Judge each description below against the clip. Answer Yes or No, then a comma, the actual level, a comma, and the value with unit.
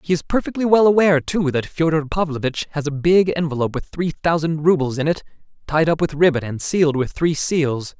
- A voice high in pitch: No, medium, 155 Hz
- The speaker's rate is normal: No, fast, 210 wpm